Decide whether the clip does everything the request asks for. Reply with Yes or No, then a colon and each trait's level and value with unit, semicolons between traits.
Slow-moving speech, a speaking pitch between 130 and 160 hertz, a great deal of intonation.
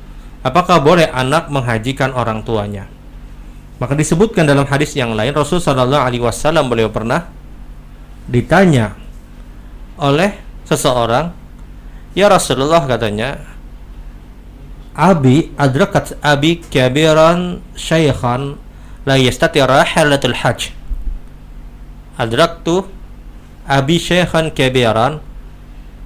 Yes: slow, 80 wpm; medium, 140 Hz; wide, 6.0 semitones